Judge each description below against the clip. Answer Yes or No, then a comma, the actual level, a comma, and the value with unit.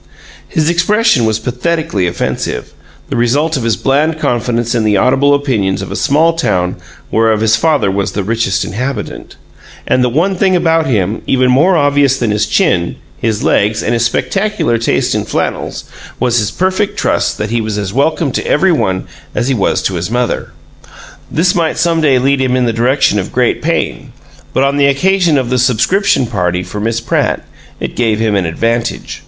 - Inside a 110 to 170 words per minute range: No, average, 190 wpm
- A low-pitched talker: Yes, low, 125 Hz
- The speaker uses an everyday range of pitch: No, wide, 5.9 semitones